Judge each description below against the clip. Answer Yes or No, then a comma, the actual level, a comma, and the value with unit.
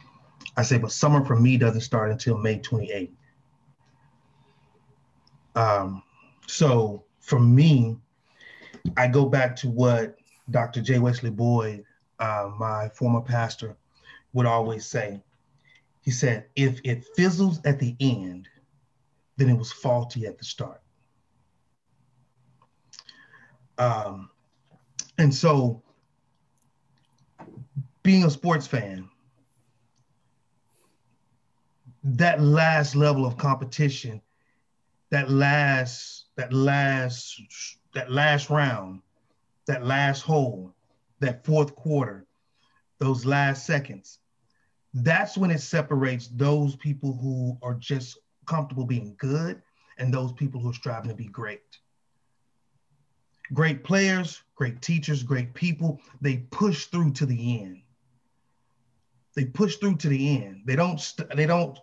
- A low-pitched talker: Yes, low, 130 Hz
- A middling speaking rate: No, slow, 115 wpm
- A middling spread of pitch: Yes, average, 3.0 semitones